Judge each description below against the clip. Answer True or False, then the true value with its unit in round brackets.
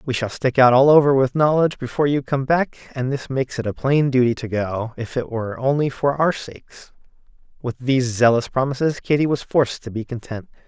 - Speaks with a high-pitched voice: False (130 Hz)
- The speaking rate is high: True (215 wpm)